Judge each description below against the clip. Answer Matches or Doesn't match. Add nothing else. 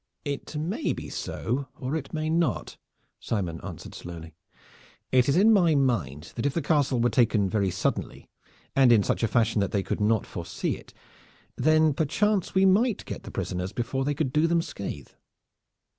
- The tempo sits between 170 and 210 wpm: Matches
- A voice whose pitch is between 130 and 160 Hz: Matches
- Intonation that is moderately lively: Doesn't match